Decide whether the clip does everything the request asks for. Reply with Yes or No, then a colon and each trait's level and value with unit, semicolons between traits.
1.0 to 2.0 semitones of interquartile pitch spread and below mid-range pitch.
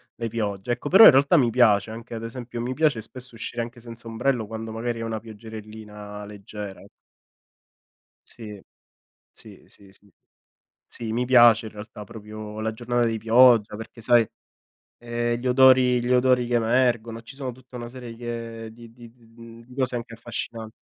Yes: narrow, 1.7 semitones; low, 115 Hz